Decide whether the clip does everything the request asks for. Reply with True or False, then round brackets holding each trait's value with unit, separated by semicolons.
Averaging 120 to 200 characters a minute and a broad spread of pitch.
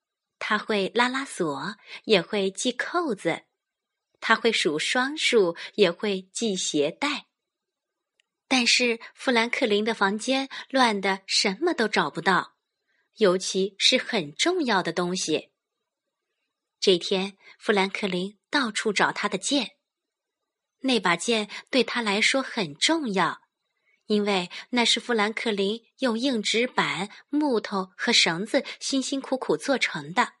False (180 characters per minute; 4.6 semitones)